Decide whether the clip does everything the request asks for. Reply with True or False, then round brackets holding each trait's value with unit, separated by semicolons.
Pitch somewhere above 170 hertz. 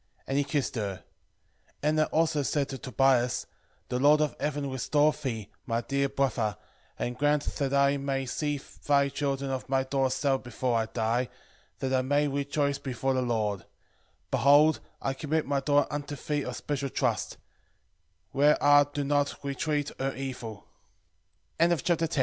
False (140 Hz)